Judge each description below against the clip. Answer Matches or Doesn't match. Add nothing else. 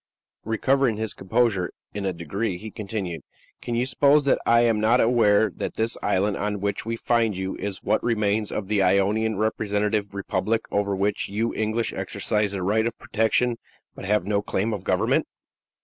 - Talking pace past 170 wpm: Matches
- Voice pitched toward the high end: Doesn't match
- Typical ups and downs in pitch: Doesn't match